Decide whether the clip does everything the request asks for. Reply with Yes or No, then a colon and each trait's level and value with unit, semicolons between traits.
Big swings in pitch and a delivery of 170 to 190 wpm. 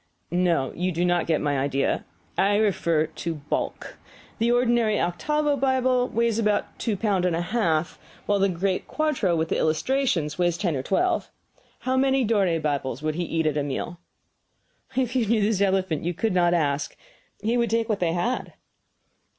Yes: wide, 6.0 semitones; average, 180 wpm